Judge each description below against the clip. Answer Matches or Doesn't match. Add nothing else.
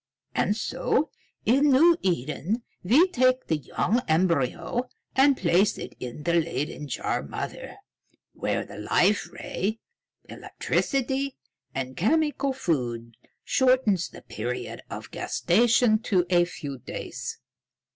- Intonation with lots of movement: Matches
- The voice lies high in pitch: Matches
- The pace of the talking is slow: Matches